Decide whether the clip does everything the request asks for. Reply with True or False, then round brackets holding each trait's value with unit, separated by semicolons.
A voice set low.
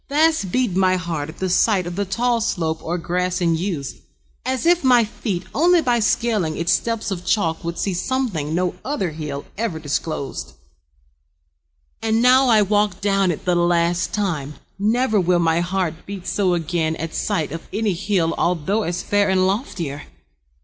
False (185 Hz)